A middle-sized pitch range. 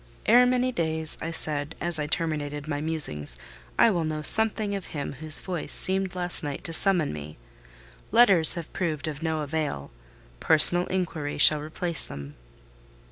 Yes: average, 3.4 semitones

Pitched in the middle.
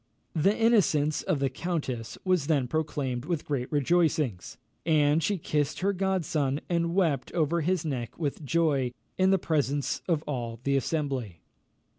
Yes: medium, 150 Hz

